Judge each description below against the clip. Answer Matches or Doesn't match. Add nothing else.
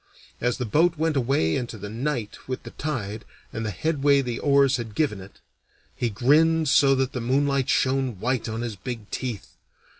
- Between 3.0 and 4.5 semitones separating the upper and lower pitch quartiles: Matches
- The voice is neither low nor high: Doesn't match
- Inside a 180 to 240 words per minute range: Matches